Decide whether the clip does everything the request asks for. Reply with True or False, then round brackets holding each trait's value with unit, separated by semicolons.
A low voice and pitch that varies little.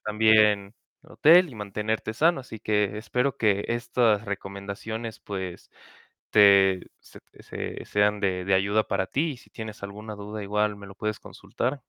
True (105 Hz; 2.0 semitones)